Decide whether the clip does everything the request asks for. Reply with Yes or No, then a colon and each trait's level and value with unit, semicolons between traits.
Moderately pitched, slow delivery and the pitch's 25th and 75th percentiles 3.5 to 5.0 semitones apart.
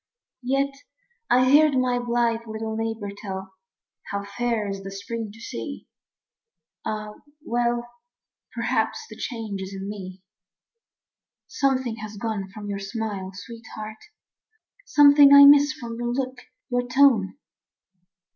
No: high, 230 Hz; slow, 125 wpm; average, 3.8 semitones